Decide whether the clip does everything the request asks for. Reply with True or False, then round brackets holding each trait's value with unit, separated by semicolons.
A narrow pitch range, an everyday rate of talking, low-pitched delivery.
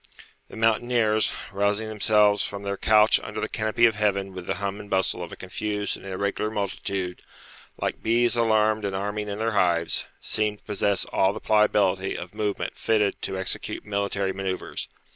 True (1.8 semitones; 175 wpm; 105 Hz)